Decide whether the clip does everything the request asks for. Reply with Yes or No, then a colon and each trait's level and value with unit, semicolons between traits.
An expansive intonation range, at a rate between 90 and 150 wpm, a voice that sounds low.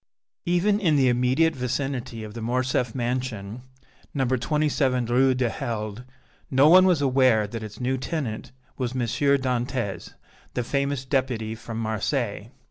No: average, 2.9 semitones; average, 140 wpm; low, 125 Hz